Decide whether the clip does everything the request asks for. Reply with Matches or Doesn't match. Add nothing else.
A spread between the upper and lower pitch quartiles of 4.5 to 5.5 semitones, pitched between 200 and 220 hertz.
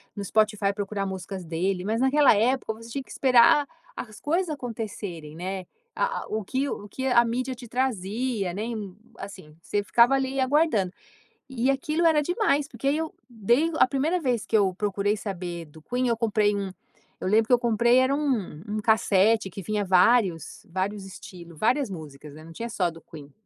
Matches